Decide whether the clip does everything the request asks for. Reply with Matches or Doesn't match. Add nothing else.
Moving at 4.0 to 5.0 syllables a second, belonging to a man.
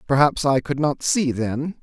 Matches